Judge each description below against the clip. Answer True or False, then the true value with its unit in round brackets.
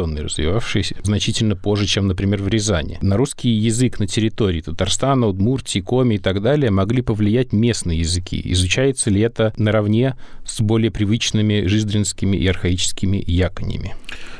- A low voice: True (105 Hz)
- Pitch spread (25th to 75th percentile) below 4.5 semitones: True (3.3 semitones)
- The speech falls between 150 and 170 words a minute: False (140 wpm)